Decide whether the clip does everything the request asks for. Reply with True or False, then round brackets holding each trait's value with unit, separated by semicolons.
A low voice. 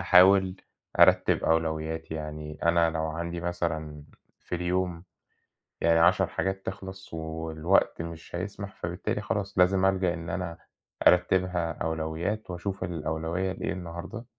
True (85 Hz)